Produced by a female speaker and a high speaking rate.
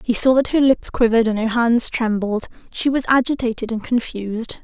No: female; average, 195 wpm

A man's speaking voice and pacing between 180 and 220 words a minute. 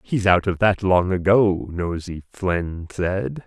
No: male; average, 155 wpm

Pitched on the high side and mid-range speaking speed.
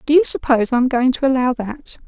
No: very high, 260 Hz; fast, 230 wpm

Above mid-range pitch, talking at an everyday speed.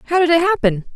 No: very high, 300 Hz; fast, 250 wpm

